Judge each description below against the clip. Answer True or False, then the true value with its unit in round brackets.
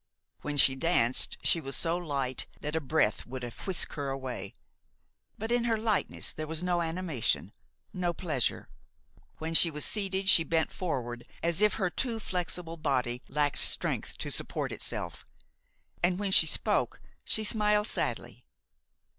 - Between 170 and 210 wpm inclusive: False (155 wpm)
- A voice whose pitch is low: False (165 Hz)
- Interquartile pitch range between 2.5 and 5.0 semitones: False (5.5 semitones)